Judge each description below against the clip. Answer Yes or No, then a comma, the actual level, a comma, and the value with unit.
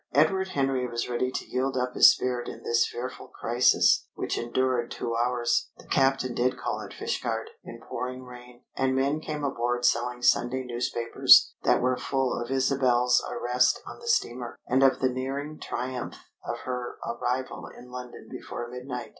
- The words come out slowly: No, average, 170 wpm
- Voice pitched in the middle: No, low, 125 Hz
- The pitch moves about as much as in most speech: No, narrow, 1.4 semitones